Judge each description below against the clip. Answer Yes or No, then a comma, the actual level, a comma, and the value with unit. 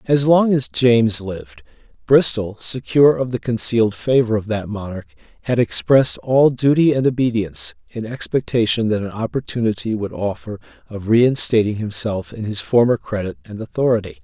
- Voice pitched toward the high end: No, low, 115 Hz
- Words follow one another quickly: No, average, 150 wpm